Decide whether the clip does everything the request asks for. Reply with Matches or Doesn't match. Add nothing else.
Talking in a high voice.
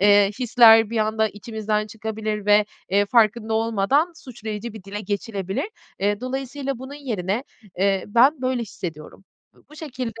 Matches